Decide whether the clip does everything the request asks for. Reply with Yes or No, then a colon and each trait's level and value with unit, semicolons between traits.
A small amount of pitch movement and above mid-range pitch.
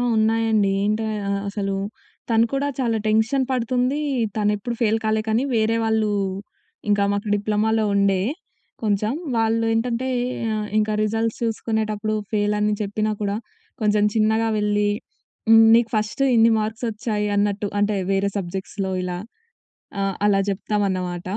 Yes: narrow, 1.5 semitones; high, 215 Hz